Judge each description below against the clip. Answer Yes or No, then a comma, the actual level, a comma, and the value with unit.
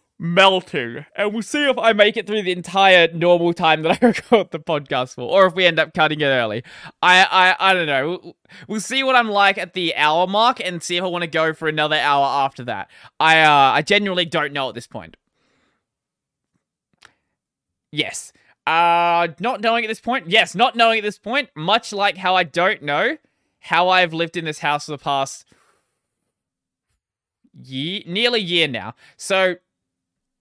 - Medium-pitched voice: Yes, medium, 175 Hz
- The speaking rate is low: No, average, 190 wpm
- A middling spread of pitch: Yes, average, 4.7 semitones